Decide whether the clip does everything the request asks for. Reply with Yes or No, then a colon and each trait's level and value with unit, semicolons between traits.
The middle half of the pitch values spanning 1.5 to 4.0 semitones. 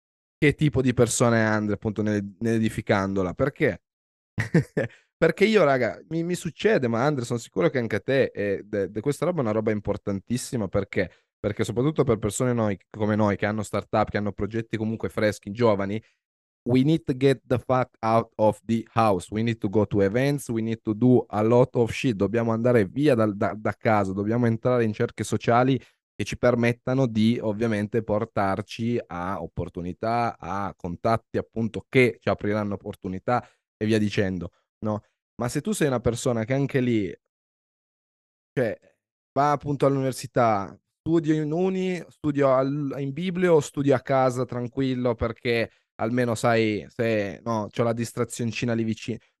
Yes: average, 3.4 semitones